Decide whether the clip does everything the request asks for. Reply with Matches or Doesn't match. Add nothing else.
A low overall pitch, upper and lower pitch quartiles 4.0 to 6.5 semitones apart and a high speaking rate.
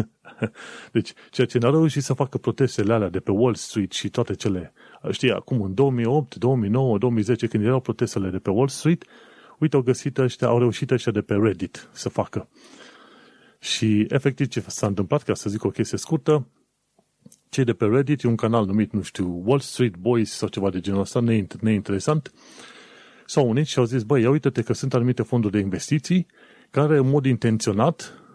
Matches